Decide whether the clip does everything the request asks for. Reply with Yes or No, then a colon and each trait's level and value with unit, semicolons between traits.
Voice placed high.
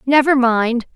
Yes: very high, 255 Hz